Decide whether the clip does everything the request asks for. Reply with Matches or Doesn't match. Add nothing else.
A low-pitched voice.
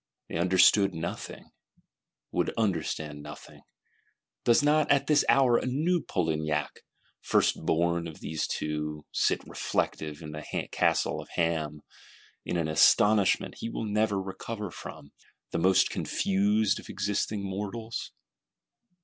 Matches